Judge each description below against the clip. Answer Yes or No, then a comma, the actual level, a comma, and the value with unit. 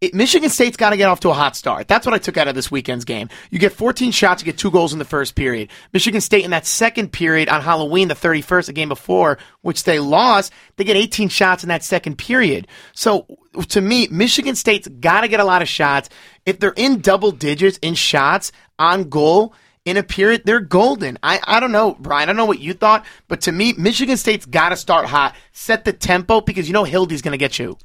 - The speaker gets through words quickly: Yes, fast, 245 wpm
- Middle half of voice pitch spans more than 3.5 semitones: Yes, average, 5.1 semitones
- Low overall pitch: No, medium, 185 Hz